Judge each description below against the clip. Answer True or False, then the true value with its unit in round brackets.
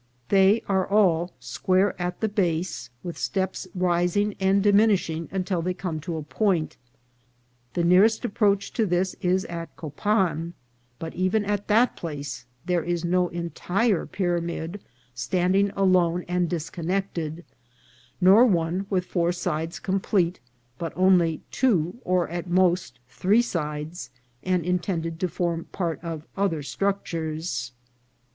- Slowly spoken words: True (130 wpm)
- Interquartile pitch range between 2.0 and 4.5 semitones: True (2.6 semitones)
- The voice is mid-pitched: True (180 Hz)